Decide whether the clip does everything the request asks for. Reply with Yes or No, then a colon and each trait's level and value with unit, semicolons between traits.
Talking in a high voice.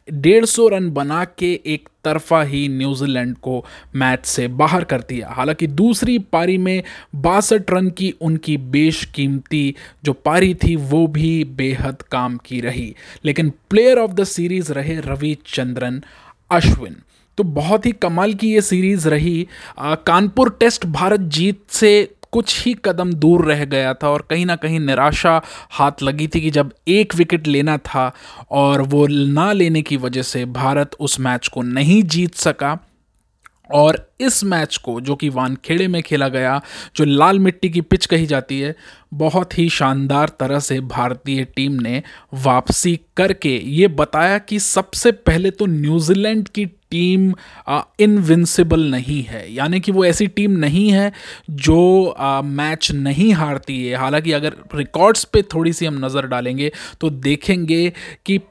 No: medium, 155 Hz